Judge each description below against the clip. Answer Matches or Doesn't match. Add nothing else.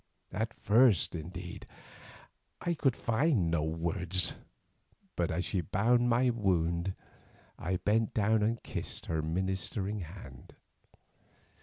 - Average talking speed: Doesn't match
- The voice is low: Matches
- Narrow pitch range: Doesn't match